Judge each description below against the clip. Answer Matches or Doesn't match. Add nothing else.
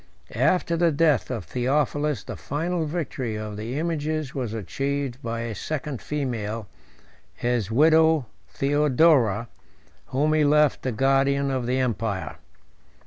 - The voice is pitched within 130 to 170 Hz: Matches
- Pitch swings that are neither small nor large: Matches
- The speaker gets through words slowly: Matches